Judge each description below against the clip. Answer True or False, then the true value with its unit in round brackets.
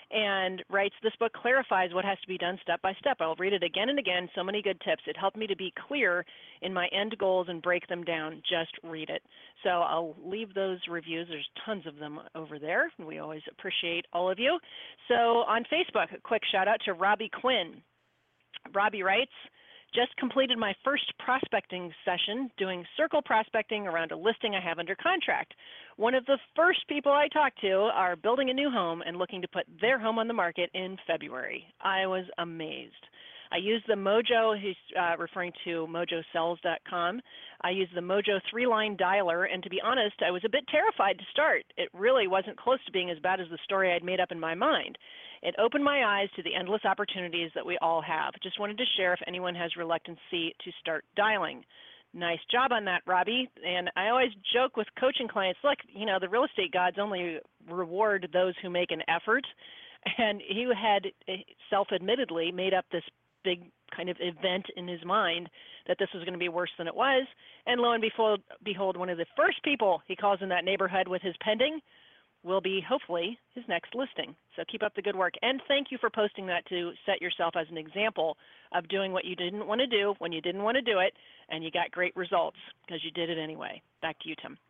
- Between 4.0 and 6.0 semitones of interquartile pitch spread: True (4.5 semitones)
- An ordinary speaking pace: False (215 wpm)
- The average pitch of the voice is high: True (195 Hz)